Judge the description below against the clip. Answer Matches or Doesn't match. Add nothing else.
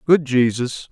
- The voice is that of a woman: Doesn't match